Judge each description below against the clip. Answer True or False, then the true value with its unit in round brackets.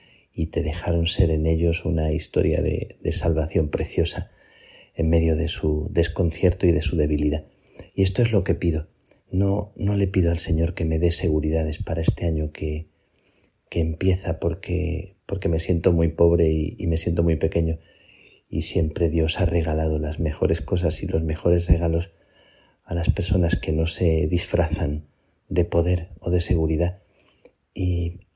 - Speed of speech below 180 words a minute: True (170 wpm)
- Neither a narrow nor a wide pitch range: False (1.9 semitones)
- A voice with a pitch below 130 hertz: True (85 Hz)